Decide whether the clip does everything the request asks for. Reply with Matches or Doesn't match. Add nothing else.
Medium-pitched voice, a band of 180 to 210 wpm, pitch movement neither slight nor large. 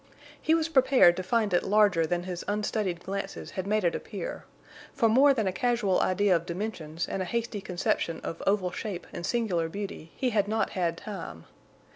Doesn't match